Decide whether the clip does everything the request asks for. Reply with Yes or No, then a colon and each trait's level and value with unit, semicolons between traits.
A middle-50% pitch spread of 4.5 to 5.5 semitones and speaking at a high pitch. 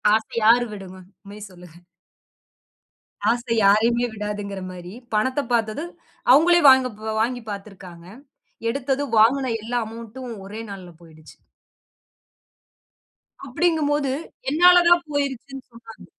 Yes: average, 5.1 semitones; high, 230 Hz